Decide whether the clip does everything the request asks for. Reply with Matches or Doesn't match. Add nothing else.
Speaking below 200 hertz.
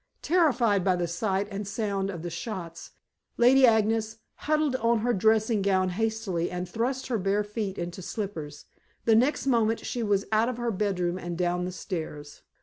Doesn't match